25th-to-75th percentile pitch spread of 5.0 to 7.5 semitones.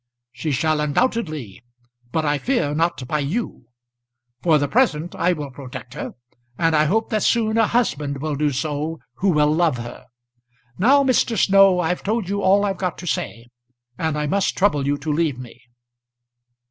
Yes: wide, 5.4 semitones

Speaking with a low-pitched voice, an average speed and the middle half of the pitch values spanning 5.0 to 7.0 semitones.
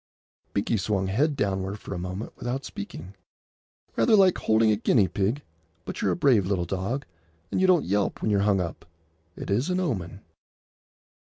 Yes: low, 105 Hz; average, 175 wpm; wide, 5.4 semitones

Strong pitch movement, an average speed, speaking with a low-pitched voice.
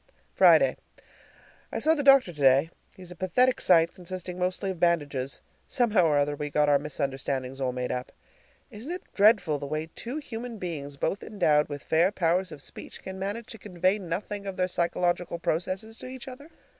No: wide, 5.8 semitones; average, 180 wpm; medium, 180 Hz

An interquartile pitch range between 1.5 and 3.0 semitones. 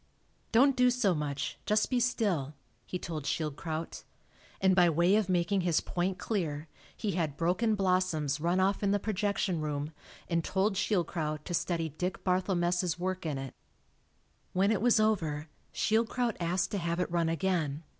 No: average, 3.7 semitones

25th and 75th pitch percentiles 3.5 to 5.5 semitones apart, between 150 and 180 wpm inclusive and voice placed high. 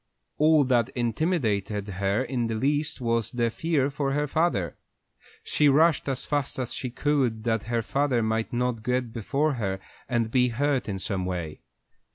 No: average, 4.2 semitones; average, 170 wpm; low, 125 Hz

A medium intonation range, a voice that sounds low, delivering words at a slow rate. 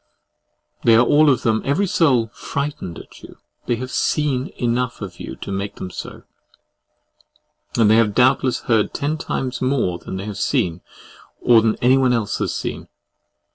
No: average, 3.9 semitones; low, 120 Hz; average, 170 wpm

